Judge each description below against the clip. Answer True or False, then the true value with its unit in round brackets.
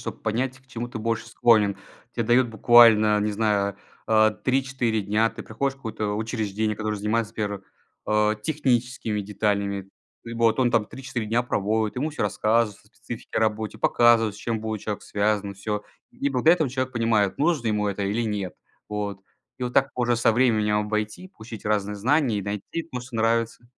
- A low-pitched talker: True (110 Hz)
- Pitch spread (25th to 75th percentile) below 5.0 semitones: True (2.4 semitones)